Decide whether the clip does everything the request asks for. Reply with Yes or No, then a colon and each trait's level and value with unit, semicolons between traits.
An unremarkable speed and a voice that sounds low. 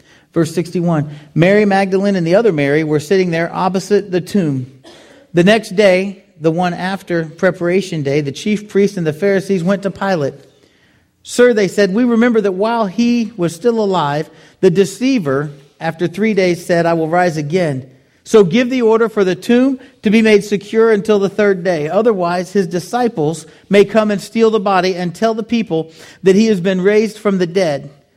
No: average, 185 wpm; high, 190 Hz